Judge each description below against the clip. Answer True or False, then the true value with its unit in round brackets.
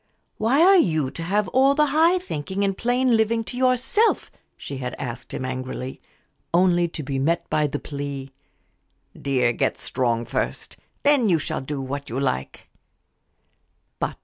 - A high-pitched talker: False (165 Hz)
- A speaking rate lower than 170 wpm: True (155 wpm)